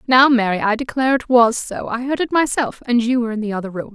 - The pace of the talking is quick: Yes, fast, 275 wpm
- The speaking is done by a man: No, female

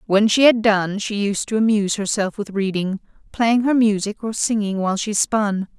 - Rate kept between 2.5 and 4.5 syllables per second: No, 4.9 syllables/s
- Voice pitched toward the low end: No, high, 210 Hz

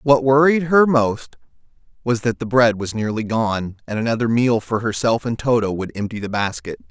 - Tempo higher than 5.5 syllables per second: No, 5.0 syllables/s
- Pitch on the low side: Yes, low, 115 Hz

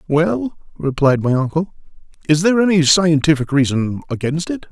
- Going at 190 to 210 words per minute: No, average, 140 wpm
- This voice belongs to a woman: No, male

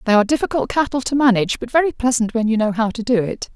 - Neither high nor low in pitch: No, high, 235 Hz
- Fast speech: Yes, fast, 270 wpm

